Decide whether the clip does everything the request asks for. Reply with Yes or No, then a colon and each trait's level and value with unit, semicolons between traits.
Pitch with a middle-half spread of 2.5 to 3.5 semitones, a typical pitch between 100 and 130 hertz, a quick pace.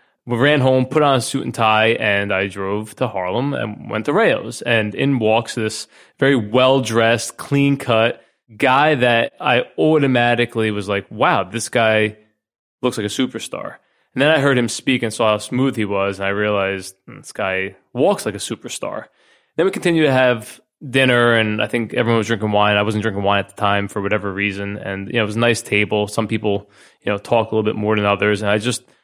Yes: average, 3.1 semitones; low, 110 Hz; fast, 215 wpm